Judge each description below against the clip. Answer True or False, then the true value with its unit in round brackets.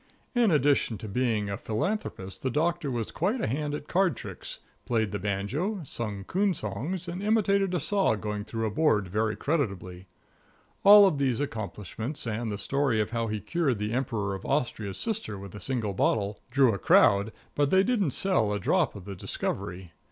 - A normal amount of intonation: False (8.3 semitones)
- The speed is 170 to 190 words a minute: True (185 wpm)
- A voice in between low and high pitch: False (120 Hz)